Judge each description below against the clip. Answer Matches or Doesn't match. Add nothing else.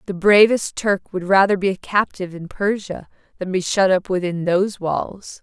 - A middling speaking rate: Matches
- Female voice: Matches